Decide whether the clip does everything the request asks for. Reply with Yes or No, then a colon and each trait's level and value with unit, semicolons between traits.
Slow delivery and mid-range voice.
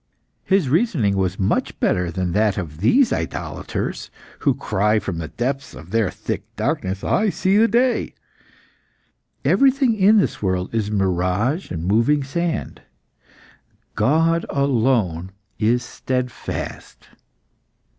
No: slow, 120 wpm; low, 115 Hz